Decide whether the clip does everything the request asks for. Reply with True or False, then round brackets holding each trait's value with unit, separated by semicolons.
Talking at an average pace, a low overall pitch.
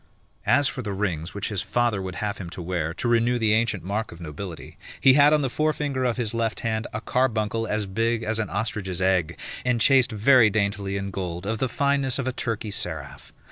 False (215 wpm; 110 Hz)